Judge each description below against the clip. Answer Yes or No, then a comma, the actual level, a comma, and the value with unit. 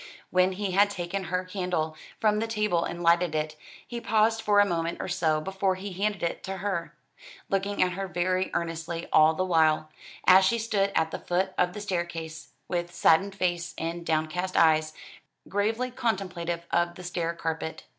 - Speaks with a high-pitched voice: No, medium, 180 Hz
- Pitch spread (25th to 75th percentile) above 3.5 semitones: No, average, 2.8 semitones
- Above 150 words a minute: Yes, average, 180 wpm